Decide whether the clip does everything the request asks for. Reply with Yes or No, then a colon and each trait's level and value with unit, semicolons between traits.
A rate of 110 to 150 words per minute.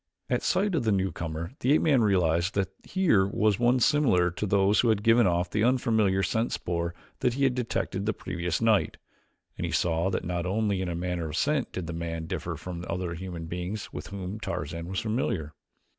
No: fast, 205 wpm